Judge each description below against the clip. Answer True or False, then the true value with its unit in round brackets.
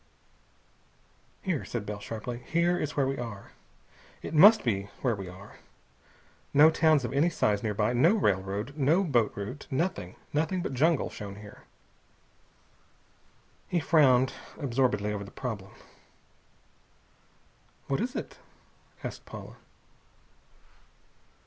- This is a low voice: True (125 Hz)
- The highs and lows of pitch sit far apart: True (7.1 semitones)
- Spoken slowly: True (120 wpm)